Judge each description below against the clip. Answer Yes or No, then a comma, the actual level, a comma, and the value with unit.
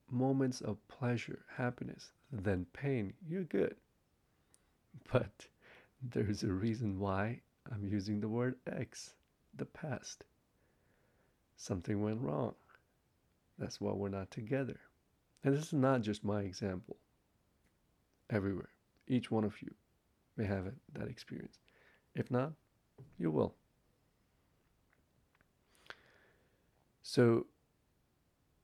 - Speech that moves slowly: Yes, slow, 105 wpm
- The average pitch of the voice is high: No, low, 110 Hz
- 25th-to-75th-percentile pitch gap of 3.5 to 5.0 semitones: Yes, average, 4.0 semitones